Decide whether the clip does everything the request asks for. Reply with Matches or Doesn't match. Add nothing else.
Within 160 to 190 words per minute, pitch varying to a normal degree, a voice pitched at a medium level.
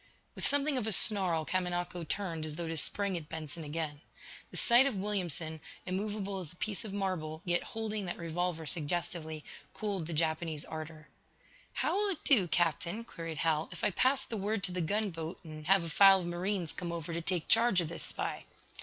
Doesn't match